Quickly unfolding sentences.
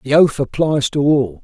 Yes: fast, 210 wpm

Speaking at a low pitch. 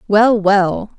No: high, 205 Hz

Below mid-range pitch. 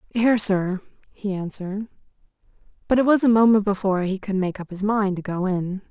No: high, 200 Hz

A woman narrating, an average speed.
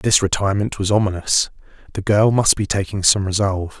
No: male; average, 175 wpm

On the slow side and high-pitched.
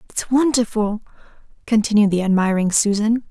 Yes: slow, 110 wpm; high, 215 Hz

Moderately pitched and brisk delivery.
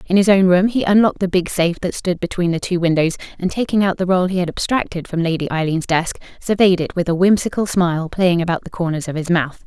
Yes: medium, 180 Hz; fast, 250 wpm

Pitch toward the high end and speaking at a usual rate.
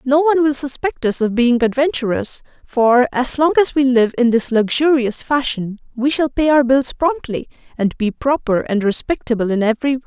Yes: very high, 260 Hz; average, 190 wpm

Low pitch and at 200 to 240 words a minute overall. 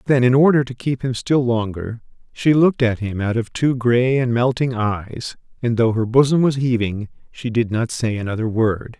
Yes: low, 120 Hz; fast, 205 wpm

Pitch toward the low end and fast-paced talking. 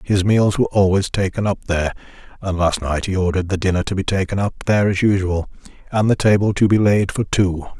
Yes: very low, 95 Hz; fast, 225 wpm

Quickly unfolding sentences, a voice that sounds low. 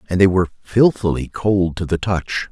No: average, 190 wpm; very low, 95 Hz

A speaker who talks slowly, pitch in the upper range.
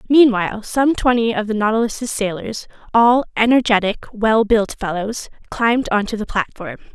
Yes: slow, 120 wpm; high, 225 Hz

